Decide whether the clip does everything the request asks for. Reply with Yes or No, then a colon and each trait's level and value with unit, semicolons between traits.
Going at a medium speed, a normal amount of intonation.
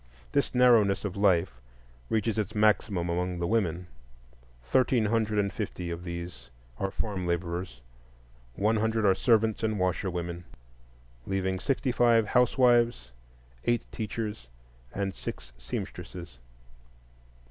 No: slow, 115 wpm; average, 4.3 semitones